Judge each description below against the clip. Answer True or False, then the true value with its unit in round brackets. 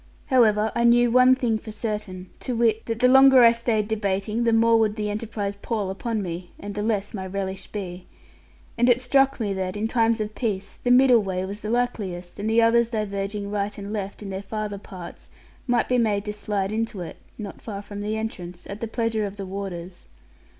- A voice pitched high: True (210 Hz)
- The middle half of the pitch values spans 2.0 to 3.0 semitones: True (2.6 semitones)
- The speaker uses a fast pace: True (215 wpm)